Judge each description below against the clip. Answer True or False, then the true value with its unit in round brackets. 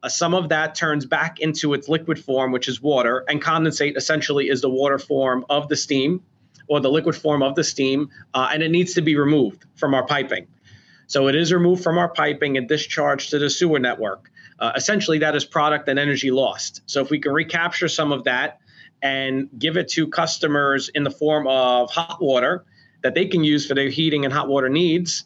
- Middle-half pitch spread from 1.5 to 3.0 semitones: True (2.6 semitones)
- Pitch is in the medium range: True (150 Hz)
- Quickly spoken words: True (215 wpm)